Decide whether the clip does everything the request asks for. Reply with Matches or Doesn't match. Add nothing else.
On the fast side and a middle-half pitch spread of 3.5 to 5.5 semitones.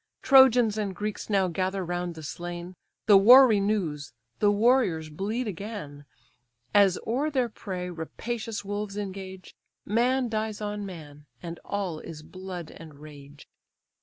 Doesn't match